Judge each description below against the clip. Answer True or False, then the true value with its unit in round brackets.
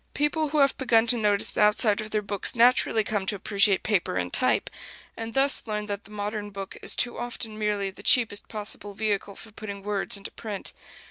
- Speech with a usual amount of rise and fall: False (2.0 semitones)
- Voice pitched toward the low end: False (210 Hz)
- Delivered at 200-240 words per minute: True (205 wpm)